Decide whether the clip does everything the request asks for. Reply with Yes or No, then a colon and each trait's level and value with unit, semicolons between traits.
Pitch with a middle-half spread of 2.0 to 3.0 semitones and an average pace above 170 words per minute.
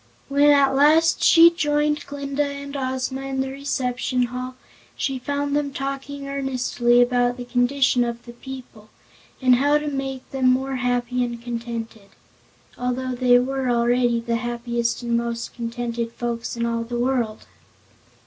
No: narrow, 2.4 semitones; average, 150 wpm